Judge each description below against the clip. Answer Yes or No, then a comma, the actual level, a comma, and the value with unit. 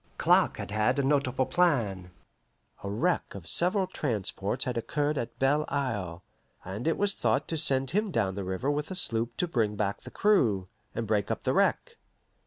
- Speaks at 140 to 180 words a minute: No, average, 190 wpm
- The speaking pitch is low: Yes, low, 125 Hz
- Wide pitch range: Yes, wide, 6.5 semitones